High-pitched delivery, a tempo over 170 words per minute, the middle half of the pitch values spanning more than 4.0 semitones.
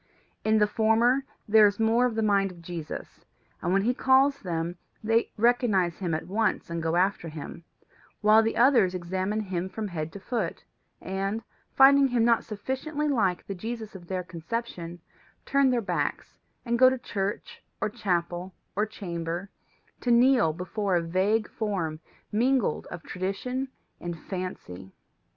No: high, 205 Hz; average, 160 wpm; average, 4.9 semitones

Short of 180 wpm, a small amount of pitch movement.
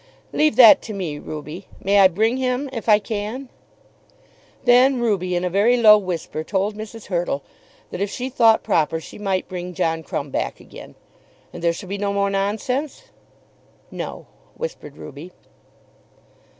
No: average, 160 wpm; average, 4.6 semitones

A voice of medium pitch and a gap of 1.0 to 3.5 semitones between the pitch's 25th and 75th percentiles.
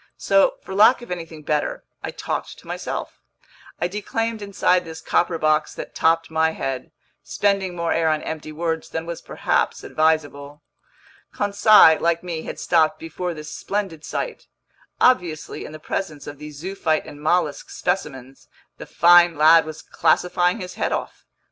Yes: medium, 165 Hz; average, 2.7 semitones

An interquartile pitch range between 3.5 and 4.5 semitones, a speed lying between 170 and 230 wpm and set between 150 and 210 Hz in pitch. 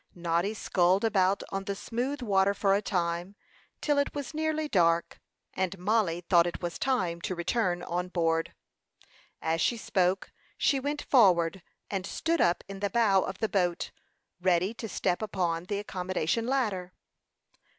No: average, 4.1 semitones; average, 160 wpm; high, 190 Hz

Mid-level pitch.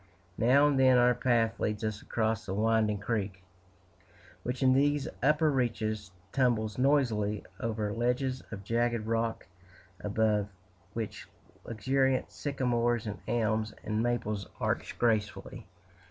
No: low, 115 Hz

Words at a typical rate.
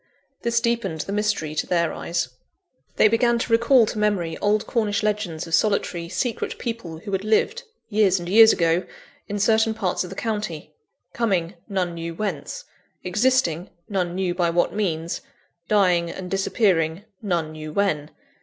Yes: average, 160 wpm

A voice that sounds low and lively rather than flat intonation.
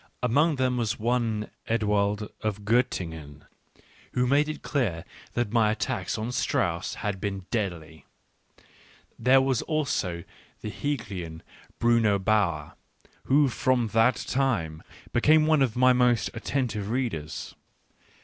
No: low, 115 Hz; average, 4.3 semitones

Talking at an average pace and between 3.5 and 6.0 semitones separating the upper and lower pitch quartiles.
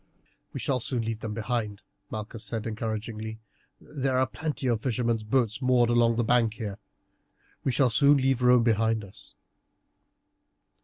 No: average, 150 wpm; narrow, 2.4 semitones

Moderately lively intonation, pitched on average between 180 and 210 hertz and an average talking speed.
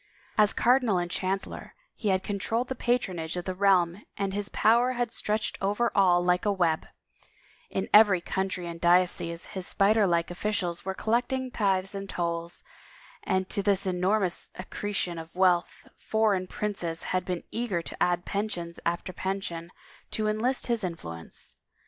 Yes: average, 3.2 semitones; high, 190 Hz; average, 160 wpm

